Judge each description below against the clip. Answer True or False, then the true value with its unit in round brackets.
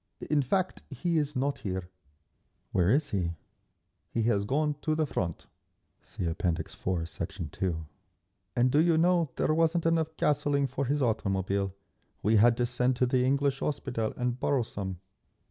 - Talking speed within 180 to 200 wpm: False (165 wpm)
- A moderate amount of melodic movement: False (7.2 semitones)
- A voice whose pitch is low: True (125 Hz)